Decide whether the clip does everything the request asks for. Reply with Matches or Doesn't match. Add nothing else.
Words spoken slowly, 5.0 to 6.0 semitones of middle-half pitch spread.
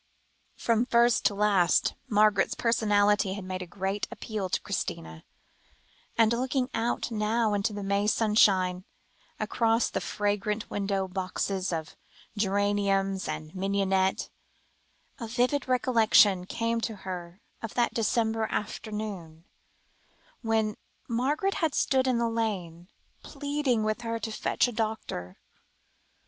Doesn't match